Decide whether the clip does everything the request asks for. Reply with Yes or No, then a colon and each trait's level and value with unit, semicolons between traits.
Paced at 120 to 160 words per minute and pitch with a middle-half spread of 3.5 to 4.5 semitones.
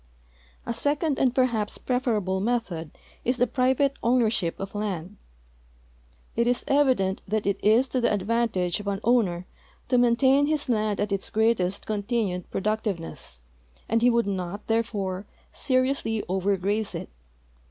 Yes: average, 150 wpm; average, 4.1 semitones